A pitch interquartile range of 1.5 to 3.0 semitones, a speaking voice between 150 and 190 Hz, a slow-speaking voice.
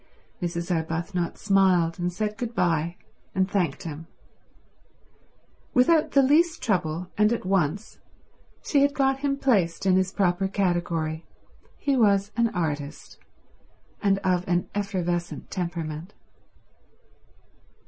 No: average, 3.8 semitones; medium, 185 Hz; slow, 115 wpm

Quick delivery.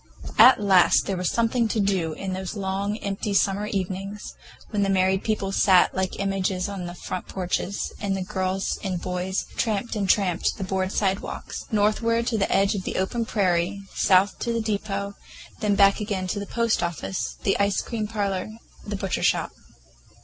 No: average, 180 wpm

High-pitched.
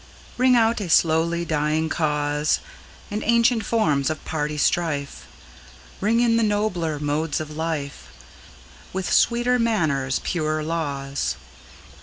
No: medium, 160 Hz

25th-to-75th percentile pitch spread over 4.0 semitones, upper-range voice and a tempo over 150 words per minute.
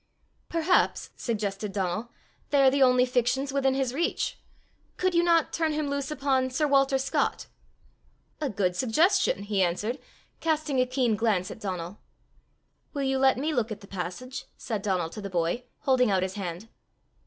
Yes: wide, 5.6 semitones; very high, 255 Hz; average, 170 wpm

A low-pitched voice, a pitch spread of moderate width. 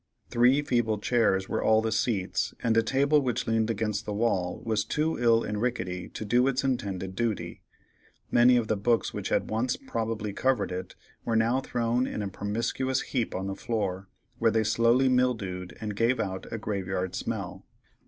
Yes: low, 115 Hz; average, 3.2 semitones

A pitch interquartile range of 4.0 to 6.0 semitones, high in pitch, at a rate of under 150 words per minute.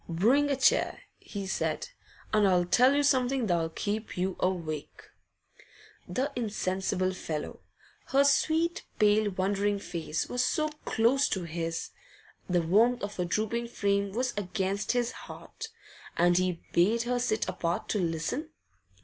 Yes: wide, 5.5 semitones; high, 205 Hz; average, 140 wpm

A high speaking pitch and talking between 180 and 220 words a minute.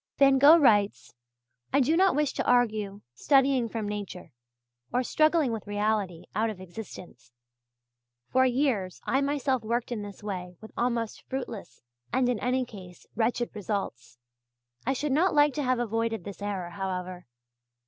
No: high, 225 Hz; average, 155 wpm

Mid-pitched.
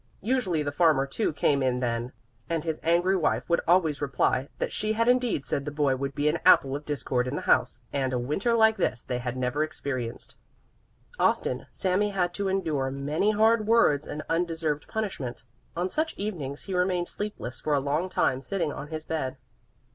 Yes: medium, 155 Hz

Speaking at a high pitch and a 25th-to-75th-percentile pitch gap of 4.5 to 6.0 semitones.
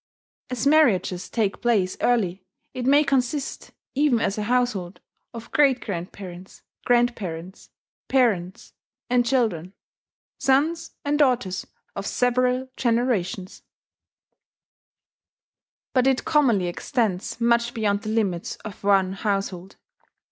Yes: high, 230 Hz; average, 4.9 semitones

